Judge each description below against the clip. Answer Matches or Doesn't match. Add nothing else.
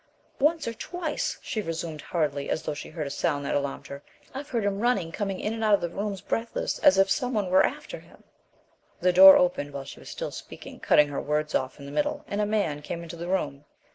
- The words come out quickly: Matches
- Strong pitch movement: Matches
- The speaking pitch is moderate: Matches